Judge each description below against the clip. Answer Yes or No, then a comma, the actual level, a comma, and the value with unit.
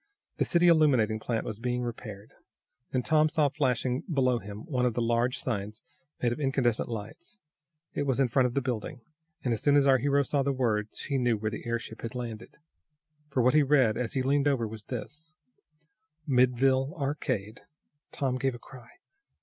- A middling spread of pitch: Yes, average, 3.2 semitones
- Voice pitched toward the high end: No, low, 125 Hz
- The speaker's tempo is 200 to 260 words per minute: No, average, 190 wpm